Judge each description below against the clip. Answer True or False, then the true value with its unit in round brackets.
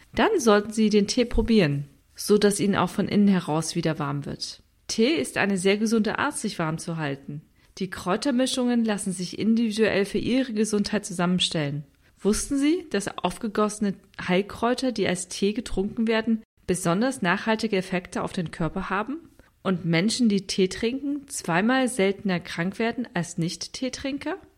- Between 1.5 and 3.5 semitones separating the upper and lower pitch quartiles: False (4.1 semitones)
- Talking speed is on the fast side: False (155 wpm)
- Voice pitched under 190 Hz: False (200 Hz)